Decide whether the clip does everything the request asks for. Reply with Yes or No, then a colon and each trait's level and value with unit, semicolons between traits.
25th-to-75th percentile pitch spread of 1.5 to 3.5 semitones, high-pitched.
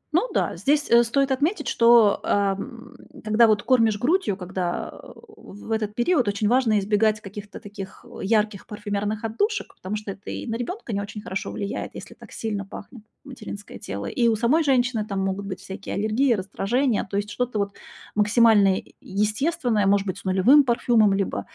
Yes: average, 3.2 semitones; high, 215 Hz